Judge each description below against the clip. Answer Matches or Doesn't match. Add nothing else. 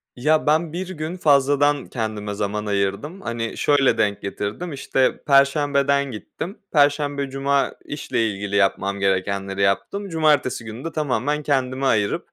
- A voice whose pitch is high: Doesn't match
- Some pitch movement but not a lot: Doesn't match